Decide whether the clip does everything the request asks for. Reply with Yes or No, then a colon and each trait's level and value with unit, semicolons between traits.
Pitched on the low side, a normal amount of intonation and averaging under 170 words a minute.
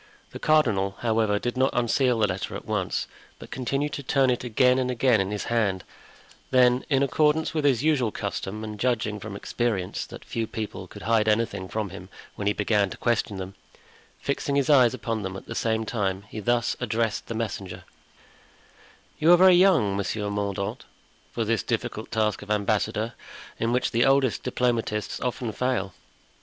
No: low, 115 Hz; average, 3.7 semitones; average, 180 wpm